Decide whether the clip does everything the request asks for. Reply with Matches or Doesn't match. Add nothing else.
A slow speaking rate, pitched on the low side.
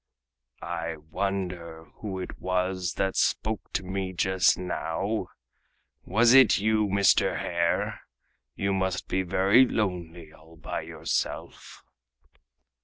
Matches